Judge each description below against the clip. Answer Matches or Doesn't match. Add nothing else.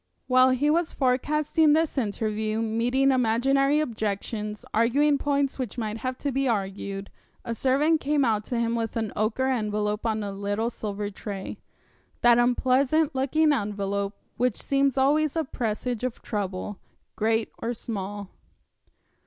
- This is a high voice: Matches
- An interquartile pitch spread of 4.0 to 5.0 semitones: Matches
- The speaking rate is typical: Matches